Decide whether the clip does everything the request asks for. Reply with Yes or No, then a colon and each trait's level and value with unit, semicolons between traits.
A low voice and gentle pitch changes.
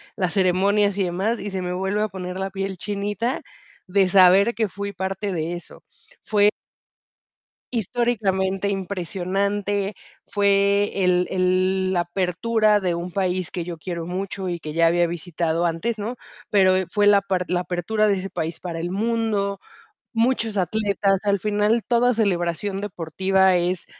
No: high, 195 Hz; narrow, 2.3 semitones